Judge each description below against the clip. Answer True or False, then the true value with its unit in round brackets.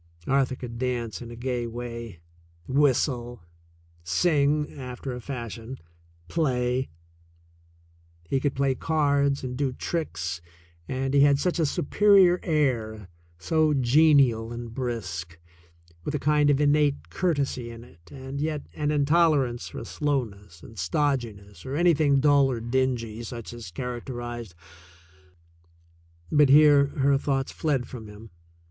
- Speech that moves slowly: True (130 wpm)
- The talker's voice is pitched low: True (130 Hz)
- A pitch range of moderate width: True (3.6 semitones)